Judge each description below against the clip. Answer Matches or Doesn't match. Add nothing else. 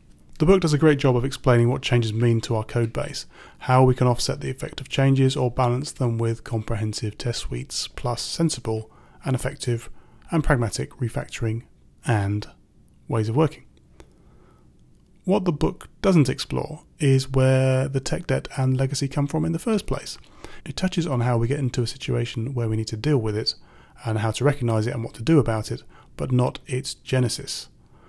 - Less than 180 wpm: Doesn't match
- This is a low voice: Matches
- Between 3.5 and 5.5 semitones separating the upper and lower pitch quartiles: Doesn't match